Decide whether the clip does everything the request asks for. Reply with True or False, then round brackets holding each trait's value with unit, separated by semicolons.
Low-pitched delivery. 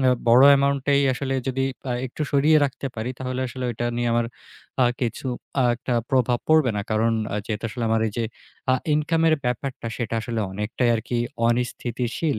True (125 Hz)